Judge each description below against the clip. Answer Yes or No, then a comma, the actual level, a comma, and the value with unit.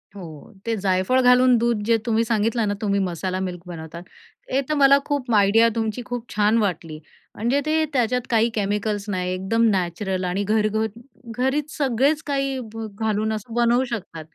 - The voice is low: No, high, 220 Hz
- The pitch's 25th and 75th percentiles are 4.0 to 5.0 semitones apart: Yes, average, 4.3 semitones